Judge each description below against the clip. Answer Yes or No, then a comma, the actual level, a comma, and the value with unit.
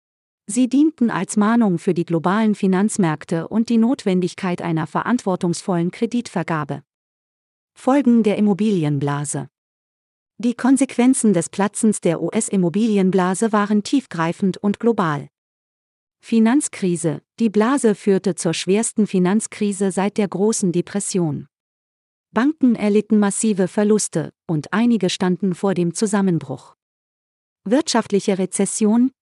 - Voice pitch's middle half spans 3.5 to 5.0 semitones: Yes, average, 4.2 semitones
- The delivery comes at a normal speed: No, slow, 105 wpm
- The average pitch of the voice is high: Yes, high, 200 Hz